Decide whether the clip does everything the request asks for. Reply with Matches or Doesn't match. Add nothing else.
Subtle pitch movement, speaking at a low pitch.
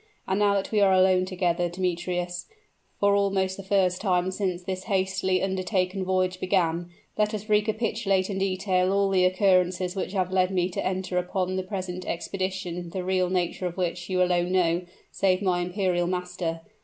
Doesn't match